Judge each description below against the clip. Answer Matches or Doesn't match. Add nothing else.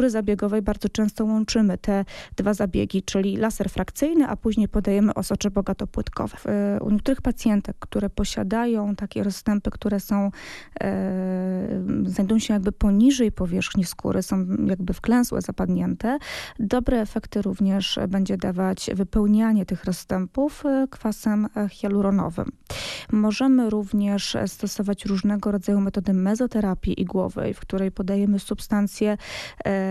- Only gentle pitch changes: Matches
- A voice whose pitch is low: Doesn't match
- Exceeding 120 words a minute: Doesn't match